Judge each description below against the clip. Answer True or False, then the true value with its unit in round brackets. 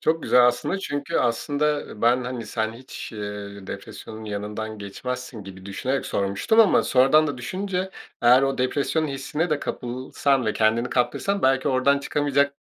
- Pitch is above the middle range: False (125 Hz)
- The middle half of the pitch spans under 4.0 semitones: False (4.6 semitones)